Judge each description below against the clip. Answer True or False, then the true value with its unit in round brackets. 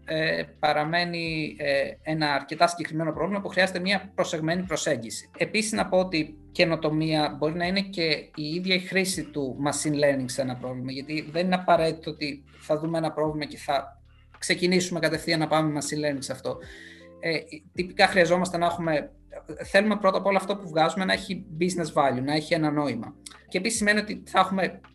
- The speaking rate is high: True (185 wpm)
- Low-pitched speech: False (160 Hz)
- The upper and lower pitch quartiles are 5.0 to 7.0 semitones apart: False (3.3 semitones)